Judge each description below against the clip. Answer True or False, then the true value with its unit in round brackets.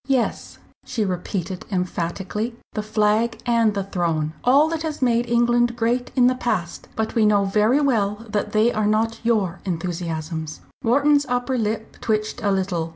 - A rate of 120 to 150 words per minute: False (160 wpm)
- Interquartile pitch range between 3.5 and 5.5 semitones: True (3.8 semitones)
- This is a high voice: True (215 Hz)